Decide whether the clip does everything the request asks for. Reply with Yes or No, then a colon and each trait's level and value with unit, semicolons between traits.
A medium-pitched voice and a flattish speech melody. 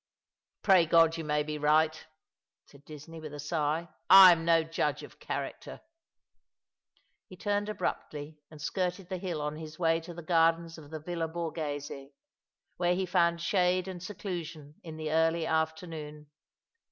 Yes: medium, 165 Hz; narrow, 2.3 semitones